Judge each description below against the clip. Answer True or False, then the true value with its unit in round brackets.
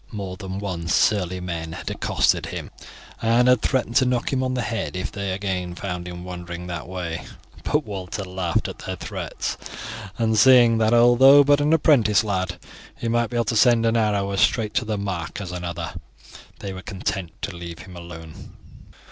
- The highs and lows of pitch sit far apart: False (4.6 semitones)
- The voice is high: False (100 Hz)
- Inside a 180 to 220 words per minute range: True (190 wpm)